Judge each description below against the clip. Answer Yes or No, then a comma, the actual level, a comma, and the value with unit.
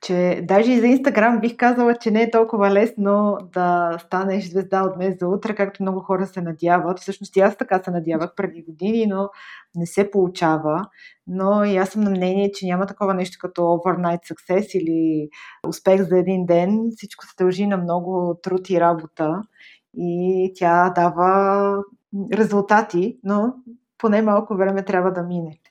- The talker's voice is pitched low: No, high, 190 Hz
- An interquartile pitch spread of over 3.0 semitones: No, narrow, 2.4 semitones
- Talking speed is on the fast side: Yes, fast, 170 wpm